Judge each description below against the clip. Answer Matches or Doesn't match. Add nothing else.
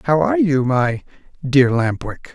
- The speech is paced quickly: Doesn't match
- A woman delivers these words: Doesn't match